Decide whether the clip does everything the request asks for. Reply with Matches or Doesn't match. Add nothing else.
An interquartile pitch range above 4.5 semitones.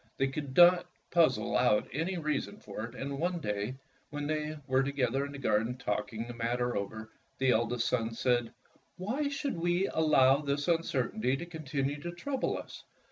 Matches